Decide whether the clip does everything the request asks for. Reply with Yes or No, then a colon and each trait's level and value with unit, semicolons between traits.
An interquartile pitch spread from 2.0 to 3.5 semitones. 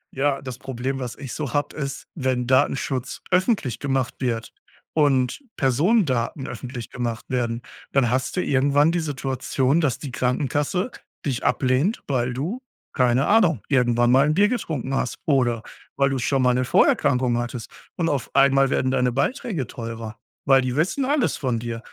Yes: average, 2.7 semitones